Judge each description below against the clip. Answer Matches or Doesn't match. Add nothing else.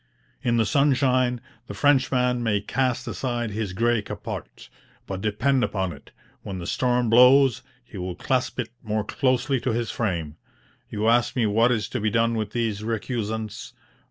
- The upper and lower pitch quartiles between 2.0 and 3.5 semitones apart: Matches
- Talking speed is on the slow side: Doesn't match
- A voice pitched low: Matches